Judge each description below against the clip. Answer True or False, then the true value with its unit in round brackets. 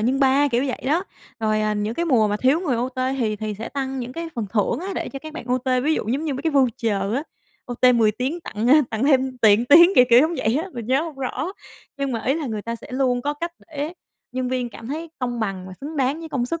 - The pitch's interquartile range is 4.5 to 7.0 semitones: False (4.0 semitones)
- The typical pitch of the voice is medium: False (255 Hz)